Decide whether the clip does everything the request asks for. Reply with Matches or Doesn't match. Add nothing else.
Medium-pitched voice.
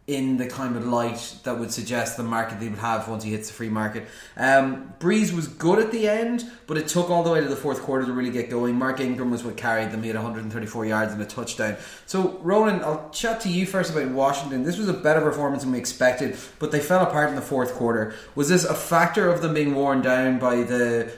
Doesn't match